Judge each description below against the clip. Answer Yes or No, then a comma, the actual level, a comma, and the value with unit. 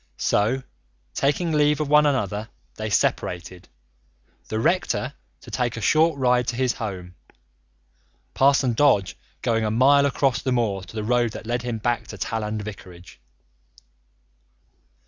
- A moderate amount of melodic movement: Yes, average, 4.2 semitones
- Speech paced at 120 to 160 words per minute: Yes, average, 145 wpm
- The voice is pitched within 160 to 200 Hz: No, low, 120 Hz